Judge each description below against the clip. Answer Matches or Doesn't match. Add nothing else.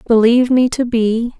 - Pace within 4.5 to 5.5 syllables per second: Matches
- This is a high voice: Matches